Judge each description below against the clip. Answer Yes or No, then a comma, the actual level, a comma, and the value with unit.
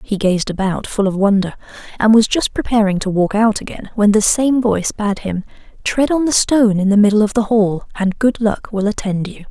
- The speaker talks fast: Yes, fast, 225 wpm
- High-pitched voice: Yes, high, 210 Hz